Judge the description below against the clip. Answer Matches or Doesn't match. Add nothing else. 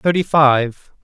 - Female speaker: Doesn't match